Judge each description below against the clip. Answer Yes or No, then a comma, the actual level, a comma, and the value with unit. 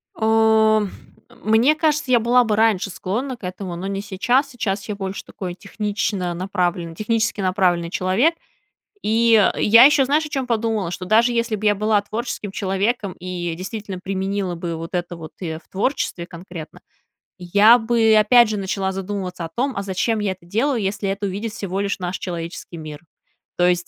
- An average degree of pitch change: Yes, average, 3.6 semitones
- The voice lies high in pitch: Yes, high, 200 Hz